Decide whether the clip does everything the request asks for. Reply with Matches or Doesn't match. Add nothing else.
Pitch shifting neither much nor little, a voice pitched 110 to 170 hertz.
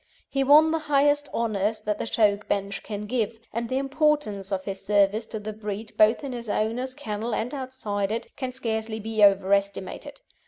Doesn't match